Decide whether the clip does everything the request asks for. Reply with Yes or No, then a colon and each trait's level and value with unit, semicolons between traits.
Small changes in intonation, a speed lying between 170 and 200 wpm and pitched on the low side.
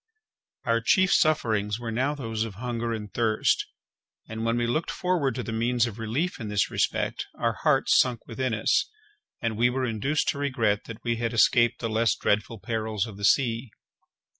Yes: narrow, 2.2 semitones; average, 190 wpm; low, 115 Hz